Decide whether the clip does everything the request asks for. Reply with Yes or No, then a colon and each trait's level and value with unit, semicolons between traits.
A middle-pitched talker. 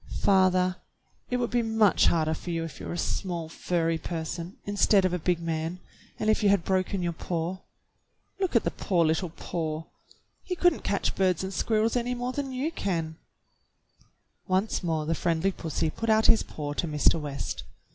Yes: medium, 180 Hz